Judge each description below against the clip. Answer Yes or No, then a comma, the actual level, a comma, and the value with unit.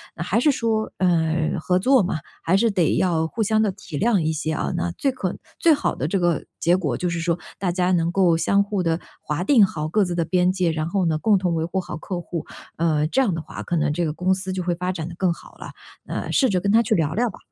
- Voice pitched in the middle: Yes, medium, 180 Hz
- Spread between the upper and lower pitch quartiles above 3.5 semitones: No, average, 3.2 semitones